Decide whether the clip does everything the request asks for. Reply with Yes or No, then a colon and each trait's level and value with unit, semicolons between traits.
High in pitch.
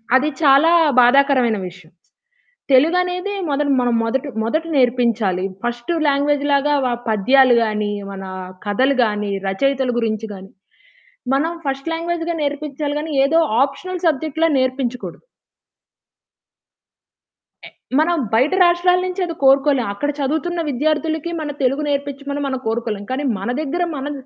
Yes: very high, 275 Hz